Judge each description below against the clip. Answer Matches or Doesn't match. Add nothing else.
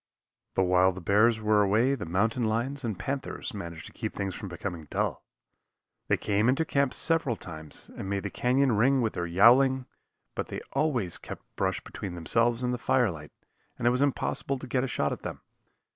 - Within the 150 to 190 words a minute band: Doesn't match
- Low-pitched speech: Matches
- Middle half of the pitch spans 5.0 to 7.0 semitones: Matches